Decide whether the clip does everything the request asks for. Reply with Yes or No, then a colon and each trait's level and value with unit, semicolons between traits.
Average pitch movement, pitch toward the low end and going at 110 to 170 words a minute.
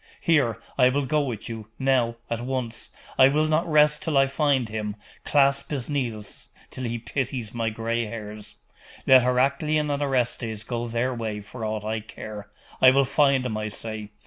No: average, 3.8 semitones; low, 125 Hz; average, 180 wpm